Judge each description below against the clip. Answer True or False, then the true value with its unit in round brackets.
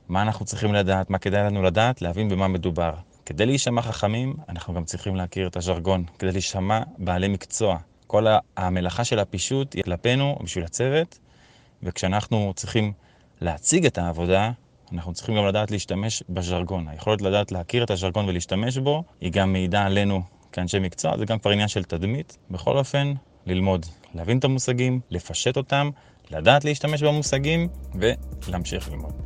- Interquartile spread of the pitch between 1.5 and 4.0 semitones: False (4.7 semitones)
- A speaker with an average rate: False (155 wpm)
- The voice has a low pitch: True (100 Hz)